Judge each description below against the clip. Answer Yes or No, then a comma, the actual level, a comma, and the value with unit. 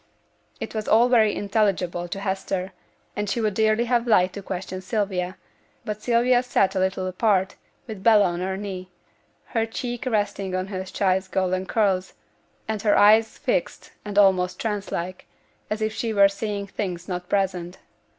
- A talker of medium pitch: No, high, 200 Hz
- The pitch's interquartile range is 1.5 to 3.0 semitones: Yes, average, 2.7 semitones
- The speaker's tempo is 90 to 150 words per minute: No, average, 170 wpm